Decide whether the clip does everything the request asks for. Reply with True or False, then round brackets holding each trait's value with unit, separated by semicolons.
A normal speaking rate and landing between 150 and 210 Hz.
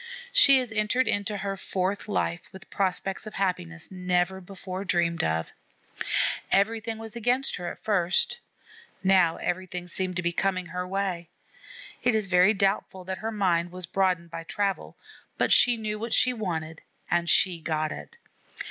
True (160 wpm; 190 Hz)